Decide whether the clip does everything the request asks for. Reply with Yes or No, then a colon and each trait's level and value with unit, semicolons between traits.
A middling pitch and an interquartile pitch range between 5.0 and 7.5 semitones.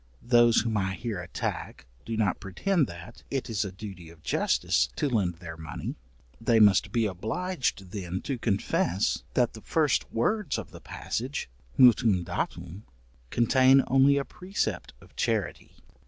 No: low, 110 Hz; wide, 5.6 semitones